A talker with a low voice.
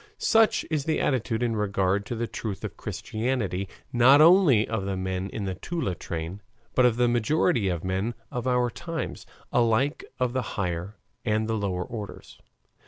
Yes: low, 110 Hz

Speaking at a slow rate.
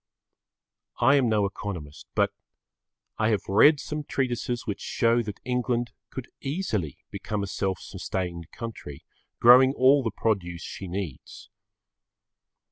Yes: slow, 125 wpm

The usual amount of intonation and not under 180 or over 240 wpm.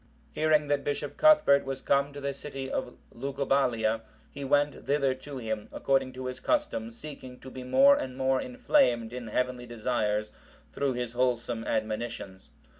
No: average, 3.0 semitones; average, 160 wpm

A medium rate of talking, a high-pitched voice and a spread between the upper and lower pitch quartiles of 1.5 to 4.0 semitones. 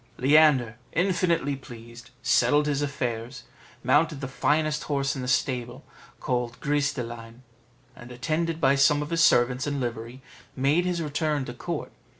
No: average, 155 wpm; medium, 140 Hz; average, 3.5 semitones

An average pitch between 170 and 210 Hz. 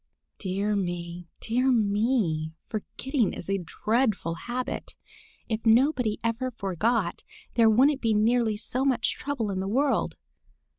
No: high, 220 Hz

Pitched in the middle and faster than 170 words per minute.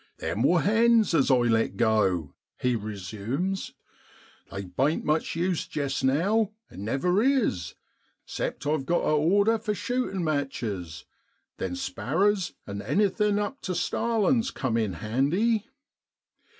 No: medium, 150 Hz; slow, 135 wpm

